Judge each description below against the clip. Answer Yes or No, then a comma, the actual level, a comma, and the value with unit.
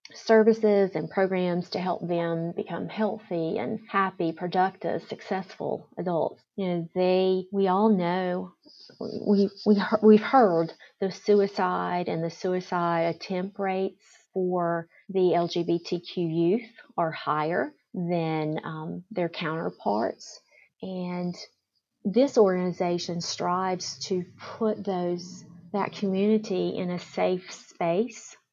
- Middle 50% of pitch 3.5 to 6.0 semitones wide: No, average, 3.0 semitones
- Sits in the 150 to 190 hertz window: Yes, medium, 185 Hz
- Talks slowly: Yes, slow, 110 wpm